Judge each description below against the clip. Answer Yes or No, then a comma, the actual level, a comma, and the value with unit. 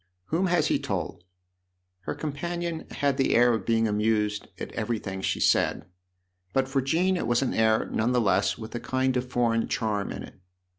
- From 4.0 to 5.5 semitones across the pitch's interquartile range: Yes, average, 4.4 semitones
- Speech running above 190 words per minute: Yes, average, 200 wpm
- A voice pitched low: Yes, low, 120 Hz